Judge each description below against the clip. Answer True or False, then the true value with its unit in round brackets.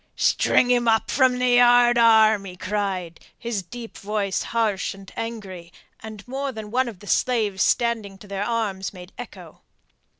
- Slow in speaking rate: False (160 wpm)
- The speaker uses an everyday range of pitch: True (3.4 semitones)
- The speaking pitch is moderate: False (220 Hz)